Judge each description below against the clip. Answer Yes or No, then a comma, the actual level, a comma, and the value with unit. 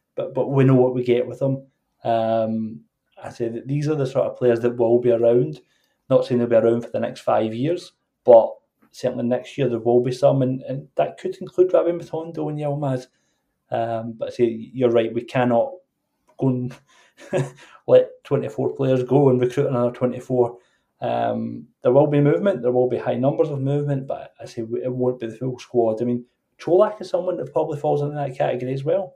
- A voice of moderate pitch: No, low, 130 Hz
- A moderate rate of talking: No, fast, 210 wpm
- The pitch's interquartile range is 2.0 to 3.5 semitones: Yes, average, 2.9 semitones